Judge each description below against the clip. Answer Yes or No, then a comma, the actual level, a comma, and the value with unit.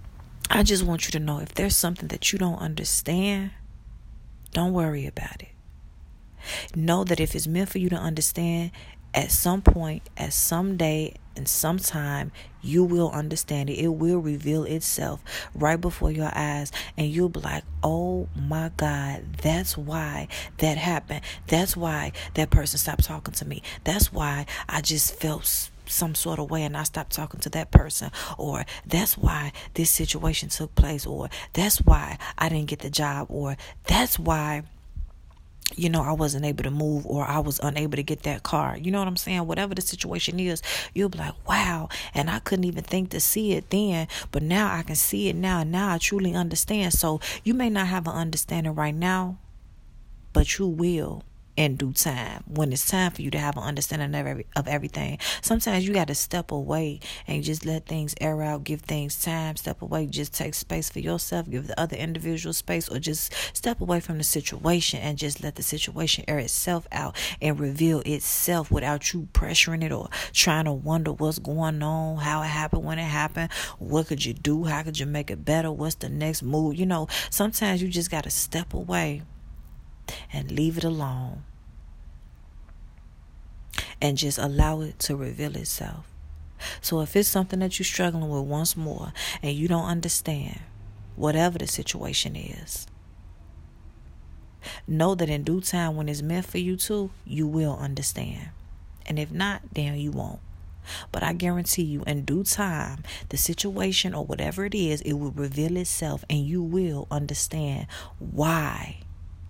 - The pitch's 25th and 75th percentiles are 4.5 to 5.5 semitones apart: No, average, 3.3 semitones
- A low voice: No, medium, 155 Hz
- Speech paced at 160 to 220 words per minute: Yes, average, 180 wpm